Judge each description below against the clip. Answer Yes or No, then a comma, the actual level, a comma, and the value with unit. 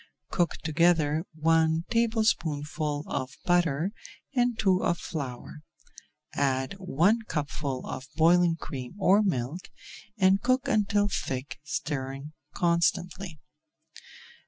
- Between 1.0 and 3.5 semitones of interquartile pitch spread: No, average, 4.6 semitones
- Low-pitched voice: No, medium, 165 Hz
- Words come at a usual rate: No, slow, 100 wpm